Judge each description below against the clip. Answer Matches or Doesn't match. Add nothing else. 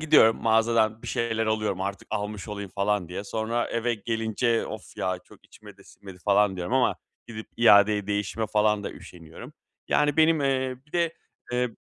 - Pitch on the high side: Doesn't match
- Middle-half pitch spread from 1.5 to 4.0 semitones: Matches